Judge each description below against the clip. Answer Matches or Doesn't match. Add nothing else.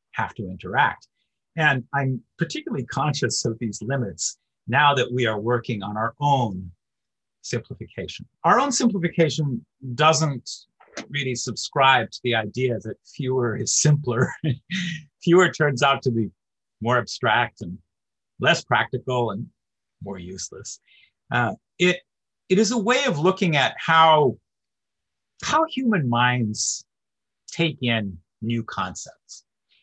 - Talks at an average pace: Doesn't match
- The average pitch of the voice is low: Matches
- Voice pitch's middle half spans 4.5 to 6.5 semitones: Matches